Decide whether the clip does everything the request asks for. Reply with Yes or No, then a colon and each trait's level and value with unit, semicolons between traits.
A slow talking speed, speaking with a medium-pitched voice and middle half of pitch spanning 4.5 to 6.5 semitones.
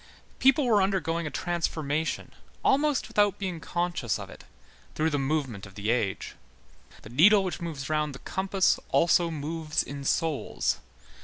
No: average, 150 wpm; medium, 160 Hz; average, 4.9 semitones